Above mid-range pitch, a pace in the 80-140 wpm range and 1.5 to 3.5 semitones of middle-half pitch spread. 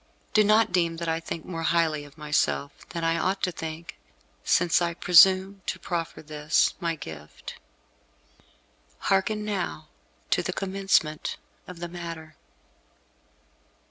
No: medium, 170 Hz; slow, 135 wpm; average, 3.0 semitones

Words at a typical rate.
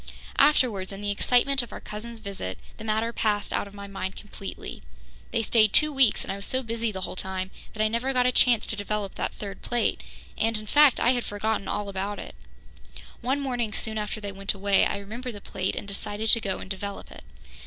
No: fast, 225 wpm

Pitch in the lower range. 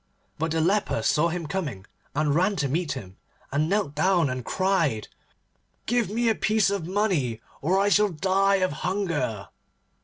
No: medium, 175 Hz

